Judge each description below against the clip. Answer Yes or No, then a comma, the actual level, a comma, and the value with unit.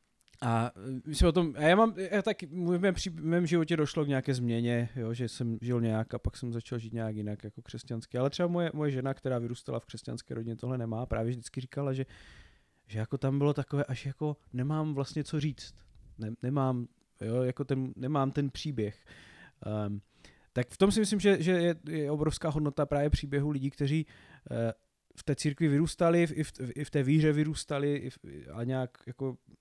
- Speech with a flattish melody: No, average, 4.5 semitones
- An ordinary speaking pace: No, fast, 210 wpm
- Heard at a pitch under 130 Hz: No, low, 135 Hz